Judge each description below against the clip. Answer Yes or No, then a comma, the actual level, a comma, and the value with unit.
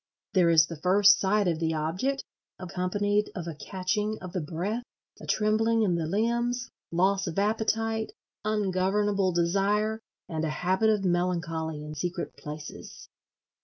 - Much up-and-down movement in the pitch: No, average, 3.8 semitones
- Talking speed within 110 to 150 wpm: Yes, average, 145 wpm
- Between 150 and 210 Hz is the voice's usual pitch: Yes, high, 190 Hz